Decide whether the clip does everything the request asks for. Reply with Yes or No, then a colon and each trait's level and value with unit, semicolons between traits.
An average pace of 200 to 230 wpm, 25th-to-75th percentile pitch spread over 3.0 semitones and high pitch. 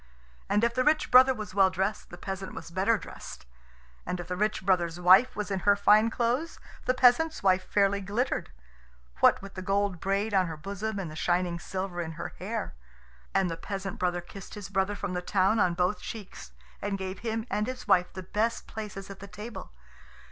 No: fast, 205 wpm; average, 2.7 semitones; high, 195 Hz